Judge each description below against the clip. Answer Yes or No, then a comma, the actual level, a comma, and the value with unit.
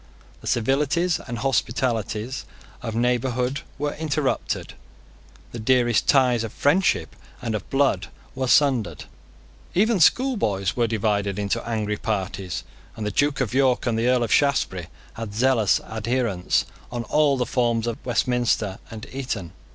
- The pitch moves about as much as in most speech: Yes, average, 3.7 semitones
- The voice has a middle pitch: No, low, 120 Hz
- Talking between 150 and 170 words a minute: No, average, 140 wpm